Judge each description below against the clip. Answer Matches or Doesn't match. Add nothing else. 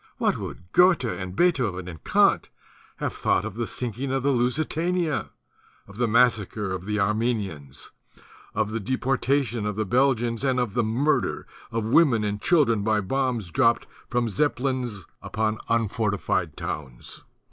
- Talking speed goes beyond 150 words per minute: Doesn't match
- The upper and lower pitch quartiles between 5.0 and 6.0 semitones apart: Doesn't match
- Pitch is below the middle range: Matches